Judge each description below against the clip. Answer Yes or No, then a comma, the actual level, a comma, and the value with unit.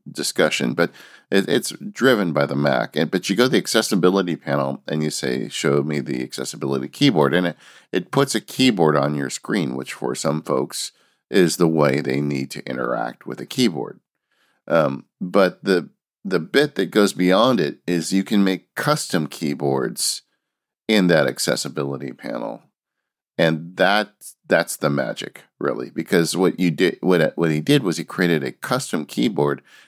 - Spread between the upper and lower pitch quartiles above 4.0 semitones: Yes, average, 4.5 semitones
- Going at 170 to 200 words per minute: Yes, average, 175 wpm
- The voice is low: Yes, very low, 75 Hz